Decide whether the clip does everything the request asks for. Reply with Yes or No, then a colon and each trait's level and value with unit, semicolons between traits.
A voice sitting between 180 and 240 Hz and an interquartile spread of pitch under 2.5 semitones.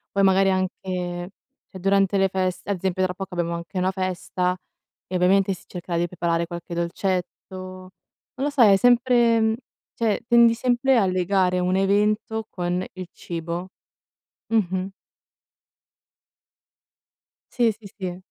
Yes: medium, 185 Hz; narrow, 2.1 semitones